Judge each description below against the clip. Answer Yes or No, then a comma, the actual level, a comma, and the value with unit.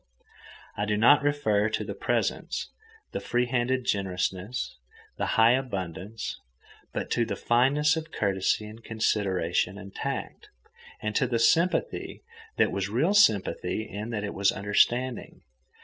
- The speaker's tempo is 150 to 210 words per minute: No, average, 140 wpm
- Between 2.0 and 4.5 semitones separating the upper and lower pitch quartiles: Yes, average, 4.0 semitones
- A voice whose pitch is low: Yes, low, 110 Hz